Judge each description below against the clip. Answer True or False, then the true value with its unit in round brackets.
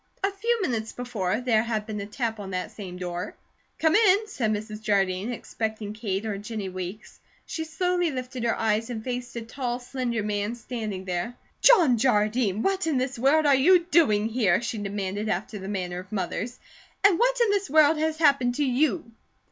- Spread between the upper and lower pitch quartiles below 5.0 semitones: False (5.5 semitones)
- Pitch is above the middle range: True (230 Hz)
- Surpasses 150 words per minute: True (190 wpm)